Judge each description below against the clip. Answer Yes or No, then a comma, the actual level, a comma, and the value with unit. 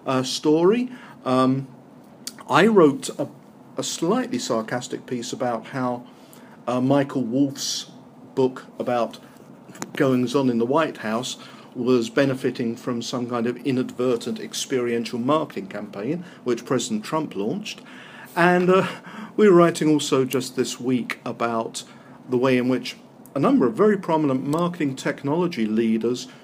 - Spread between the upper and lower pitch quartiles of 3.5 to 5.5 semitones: Yes, average, 3.8 semitones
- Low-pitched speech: Yes, low, 130 Hz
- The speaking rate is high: No, slow, 135 wpm